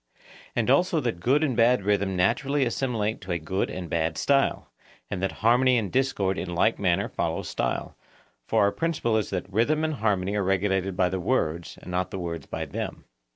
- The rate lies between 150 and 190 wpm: No, average, 200 wpm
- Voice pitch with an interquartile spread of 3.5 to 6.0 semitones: Yes, average, 5.3 semitones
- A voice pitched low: Yes, low, 100 Hz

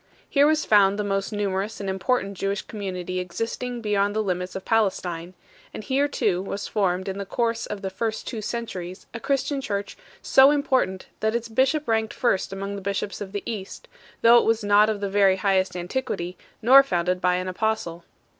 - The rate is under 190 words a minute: No, average, 195 wpm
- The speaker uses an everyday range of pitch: Yes, average, 3.2 semitones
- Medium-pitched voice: No, high, 200 Hz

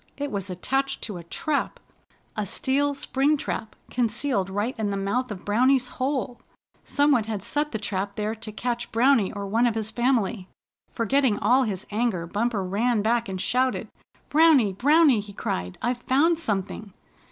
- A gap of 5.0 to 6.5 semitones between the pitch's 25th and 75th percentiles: No, average, 4.6 semitones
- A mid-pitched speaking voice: No, high, 230 Hz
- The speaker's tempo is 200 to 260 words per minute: No, average, 170 wpm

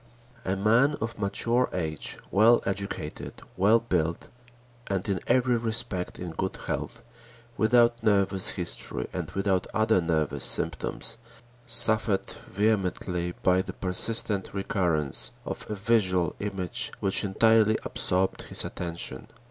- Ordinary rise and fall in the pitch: Yes, average, 3.5 semitones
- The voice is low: Yes, low, 100 Hz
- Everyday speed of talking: No, slow, 120 wpm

